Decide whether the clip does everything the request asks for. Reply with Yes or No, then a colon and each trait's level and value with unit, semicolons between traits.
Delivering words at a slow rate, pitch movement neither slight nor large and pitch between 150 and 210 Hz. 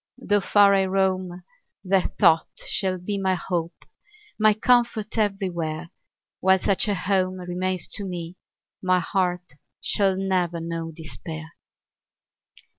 No: slow, 120 wpm; narrow, 2.0 semitones; medium, 185 Hz